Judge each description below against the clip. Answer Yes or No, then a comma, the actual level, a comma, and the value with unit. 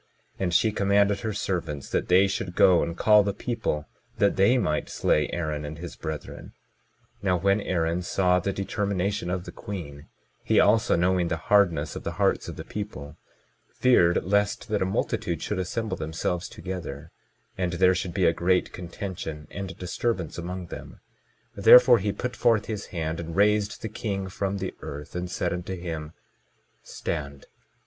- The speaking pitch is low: Yes, very low, 90 Hz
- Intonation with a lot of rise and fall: No, average, 3.3 semitones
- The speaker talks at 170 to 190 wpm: Yes, average, 175 wpm